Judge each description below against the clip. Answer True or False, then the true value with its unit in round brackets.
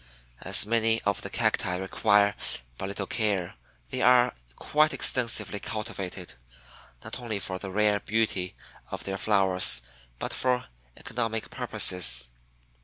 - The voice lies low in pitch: True (100 Hz)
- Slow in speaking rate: True (125 wpm)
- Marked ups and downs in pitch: False (3.0 semitones)